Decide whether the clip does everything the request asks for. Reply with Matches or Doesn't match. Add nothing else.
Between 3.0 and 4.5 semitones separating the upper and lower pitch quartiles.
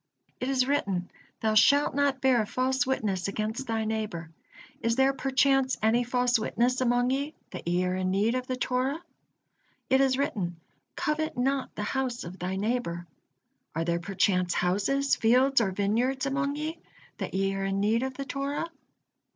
Doesn't match